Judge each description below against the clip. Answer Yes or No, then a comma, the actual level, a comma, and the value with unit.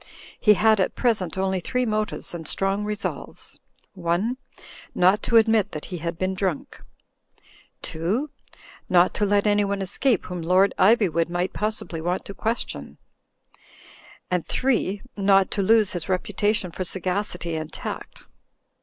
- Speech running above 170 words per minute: No, average, 140 wpm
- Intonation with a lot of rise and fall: No, average, 3.0 semitones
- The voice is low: No, high, 195 Hz